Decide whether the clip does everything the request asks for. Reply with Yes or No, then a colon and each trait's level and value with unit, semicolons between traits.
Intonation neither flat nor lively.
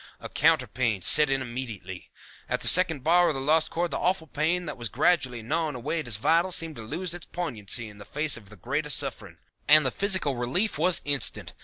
No: wide, 5.7 semitones